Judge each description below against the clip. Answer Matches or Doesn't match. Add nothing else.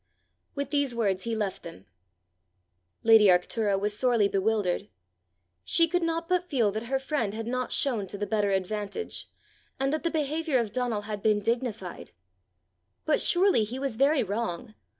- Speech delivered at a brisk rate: Doesn't match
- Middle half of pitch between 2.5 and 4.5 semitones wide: Doesn't match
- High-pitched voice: Matches